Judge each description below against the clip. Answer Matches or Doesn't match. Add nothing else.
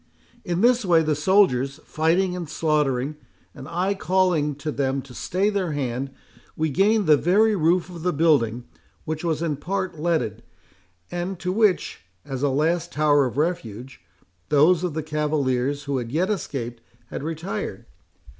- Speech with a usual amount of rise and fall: Matches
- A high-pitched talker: Doesn't match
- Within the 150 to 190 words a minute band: Matches